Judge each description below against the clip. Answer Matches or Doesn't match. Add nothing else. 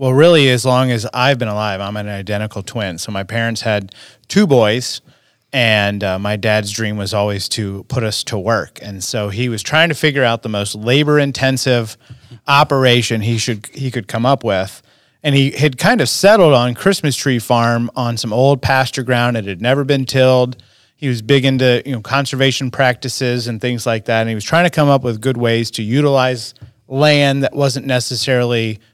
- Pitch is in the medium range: Doesn't match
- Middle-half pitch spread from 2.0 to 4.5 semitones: Matches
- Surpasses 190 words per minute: Matches